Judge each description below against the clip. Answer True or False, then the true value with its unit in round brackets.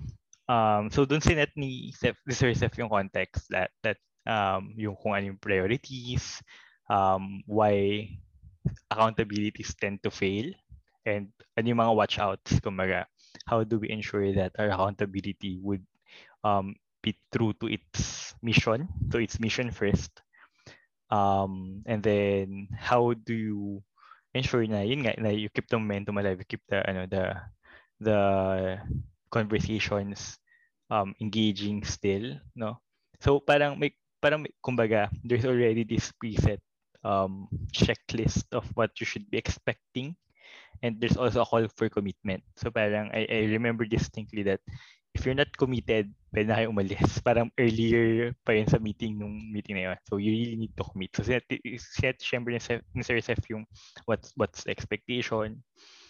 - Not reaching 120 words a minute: False (140 wpm)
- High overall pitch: False (110 Hz)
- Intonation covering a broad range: False (2.9 semitones)